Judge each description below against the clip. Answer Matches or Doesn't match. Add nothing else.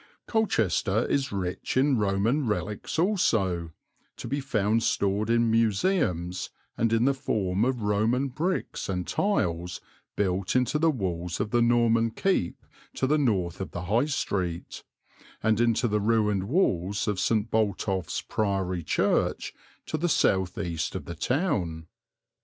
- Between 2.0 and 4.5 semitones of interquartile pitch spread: Doesn't match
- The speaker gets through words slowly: Doesn't match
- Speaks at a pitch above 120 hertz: Doesn't match